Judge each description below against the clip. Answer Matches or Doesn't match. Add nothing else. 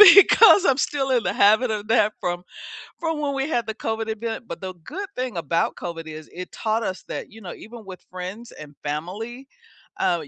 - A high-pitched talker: Matches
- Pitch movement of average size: Doesn't match